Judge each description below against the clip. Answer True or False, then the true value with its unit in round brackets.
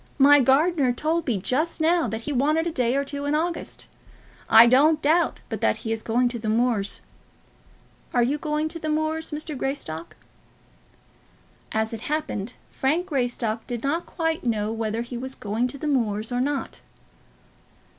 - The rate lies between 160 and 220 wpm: True (175 wpm)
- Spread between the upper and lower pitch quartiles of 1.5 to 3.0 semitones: False (4.9 semitones)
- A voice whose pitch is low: False (265 Hz)